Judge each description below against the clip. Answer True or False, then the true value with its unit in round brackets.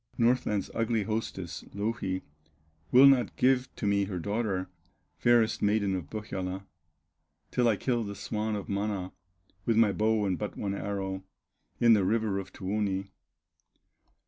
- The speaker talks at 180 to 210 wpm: False (145 wpm)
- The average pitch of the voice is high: False (105 Hz)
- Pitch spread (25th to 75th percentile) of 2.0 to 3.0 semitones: True (2.7 semitones)